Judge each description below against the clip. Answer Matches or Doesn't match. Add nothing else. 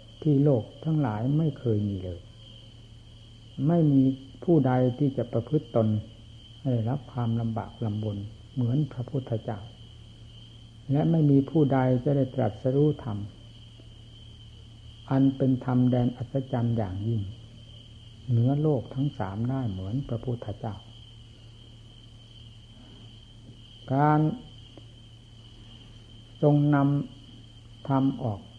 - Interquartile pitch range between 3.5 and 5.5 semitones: Doesn't match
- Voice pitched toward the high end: Doesn't match